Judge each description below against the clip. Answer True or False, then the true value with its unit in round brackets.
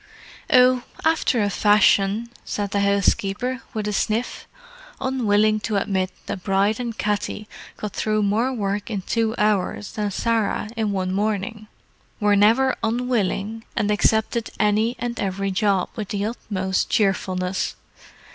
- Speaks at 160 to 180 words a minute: False (135 wpm)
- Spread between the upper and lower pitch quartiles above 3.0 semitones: False (2.4 semitones)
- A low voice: False (210 Hz)